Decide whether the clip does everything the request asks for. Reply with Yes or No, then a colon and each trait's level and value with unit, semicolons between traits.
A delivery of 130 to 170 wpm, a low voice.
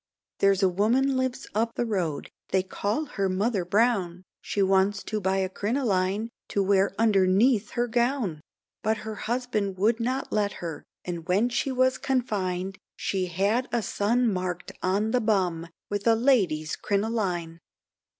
No: average, 150 wpm; high, 205 Hz